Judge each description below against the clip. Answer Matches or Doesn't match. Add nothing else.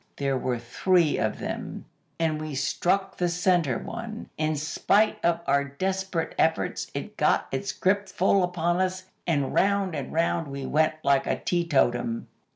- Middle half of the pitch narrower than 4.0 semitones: Doesn't match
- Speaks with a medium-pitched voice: Matches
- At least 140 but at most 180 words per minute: Matches